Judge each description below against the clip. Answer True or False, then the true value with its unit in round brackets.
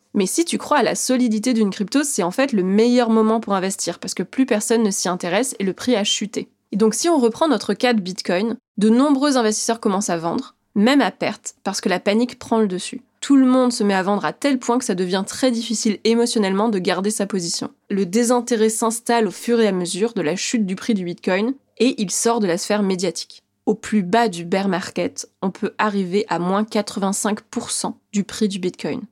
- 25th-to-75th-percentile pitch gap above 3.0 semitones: True (3.4 semitones)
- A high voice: True (215 Hz)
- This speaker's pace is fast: True (230 wpm)